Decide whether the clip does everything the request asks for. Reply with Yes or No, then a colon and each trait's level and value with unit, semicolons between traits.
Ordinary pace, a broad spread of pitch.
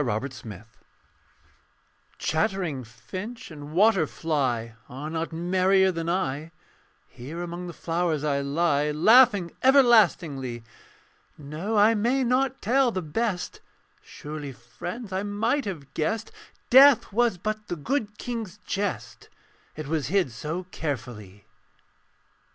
No: slow, 120 wpm; wide, 6.8 semitones